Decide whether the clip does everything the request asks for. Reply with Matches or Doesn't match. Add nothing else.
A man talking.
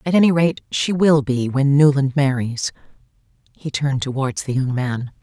Doesn't match